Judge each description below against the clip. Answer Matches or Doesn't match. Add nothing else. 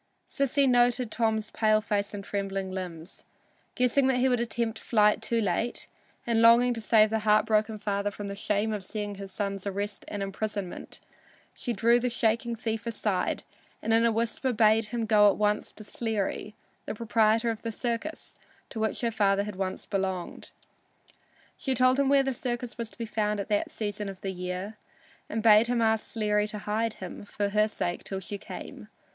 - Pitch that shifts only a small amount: Matches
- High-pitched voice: Matches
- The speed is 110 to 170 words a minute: Doesn't match